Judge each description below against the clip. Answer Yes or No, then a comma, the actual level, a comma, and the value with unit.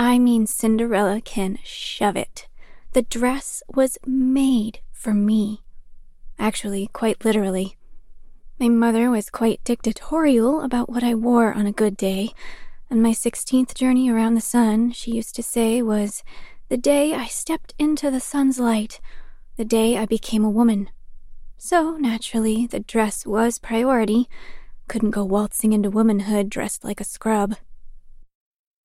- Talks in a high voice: Yes, high, 230 Hz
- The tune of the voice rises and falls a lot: No, average, 2.7 semitones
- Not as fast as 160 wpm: Yes, average, 145 wpm